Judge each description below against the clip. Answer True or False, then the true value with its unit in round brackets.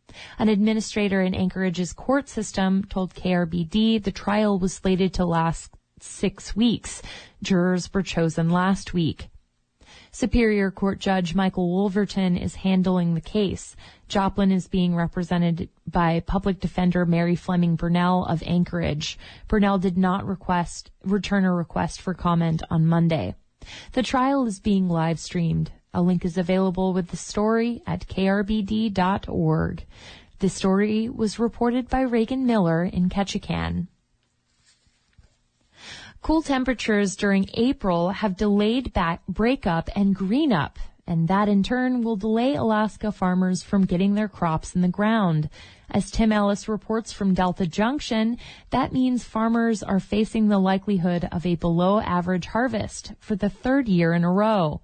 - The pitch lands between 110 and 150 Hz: False (190 Hz)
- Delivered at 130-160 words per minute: True (140 wpm)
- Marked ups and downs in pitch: False (3.5 semitones)